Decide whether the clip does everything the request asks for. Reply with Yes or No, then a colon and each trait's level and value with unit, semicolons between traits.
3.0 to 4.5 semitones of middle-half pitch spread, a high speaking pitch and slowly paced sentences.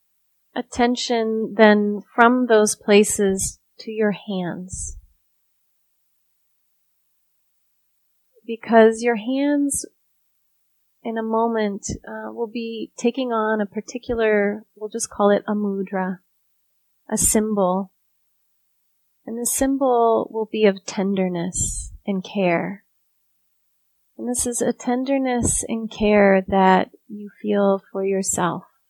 Yes: average, 3.6 semitones; high, 210 Hz; slow, 105 wpm